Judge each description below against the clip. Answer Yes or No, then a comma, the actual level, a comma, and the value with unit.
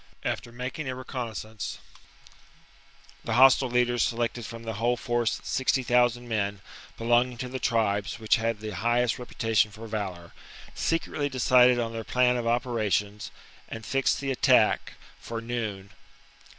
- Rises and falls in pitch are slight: Yes, narrow, 2.0 semitones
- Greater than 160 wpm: No, average, 140 wpm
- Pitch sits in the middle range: No, low, 120 Hz